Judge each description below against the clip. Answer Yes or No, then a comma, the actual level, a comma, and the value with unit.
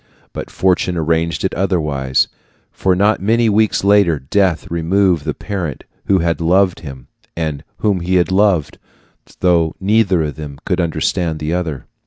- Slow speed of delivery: No, average, 155 wpm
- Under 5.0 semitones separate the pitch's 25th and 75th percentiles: Yes, average, 3.4 semitones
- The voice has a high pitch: No, very low, 90 Hz